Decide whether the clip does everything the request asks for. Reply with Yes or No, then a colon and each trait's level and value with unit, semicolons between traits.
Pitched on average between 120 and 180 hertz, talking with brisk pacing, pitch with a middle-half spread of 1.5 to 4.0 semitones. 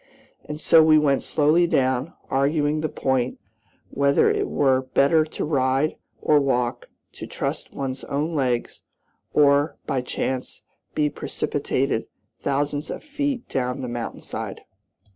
No: medium, 140 Hz; slow, 135 wpm; average, 2.7 semitones